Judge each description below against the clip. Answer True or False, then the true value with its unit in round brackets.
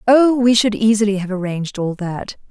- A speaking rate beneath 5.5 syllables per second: True (5.3 syllables/s)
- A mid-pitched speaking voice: False (210 Hz)